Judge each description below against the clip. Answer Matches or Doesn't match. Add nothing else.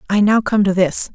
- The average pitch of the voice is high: Matches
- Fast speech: Matches